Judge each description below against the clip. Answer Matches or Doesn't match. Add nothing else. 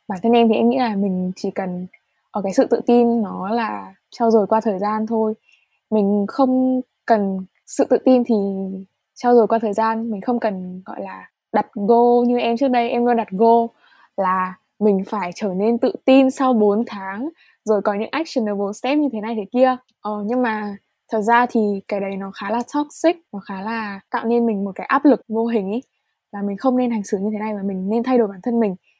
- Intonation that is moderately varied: Matches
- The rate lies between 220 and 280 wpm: Matches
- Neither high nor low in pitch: Doesn't match